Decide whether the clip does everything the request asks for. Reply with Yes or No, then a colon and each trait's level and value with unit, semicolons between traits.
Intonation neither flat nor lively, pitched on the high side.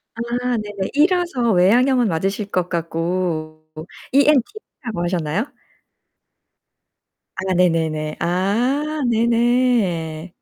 No: wide, 6.3 semitones; high, 200 Hz